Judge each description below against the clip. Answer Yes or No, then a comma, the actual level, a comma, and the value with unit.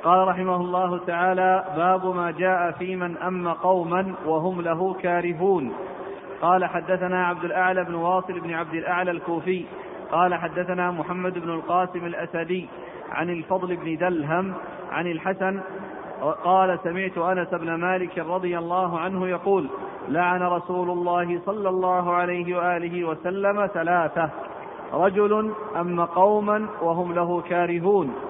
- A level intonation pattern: Yes, narrow, 1.1 semitones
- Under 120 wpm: No, average, 125 wpm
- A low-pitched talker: No, medium, 180 Hz